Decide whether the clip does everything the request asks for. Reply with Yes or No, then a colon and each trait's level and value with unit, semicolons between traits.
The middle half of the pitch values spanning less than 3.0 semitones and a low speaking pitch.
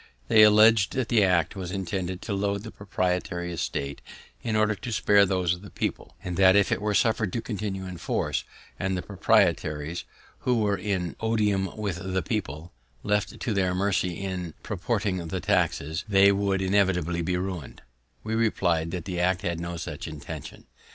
Yes: narrow, 2.6 semitones; very low, 95 Hz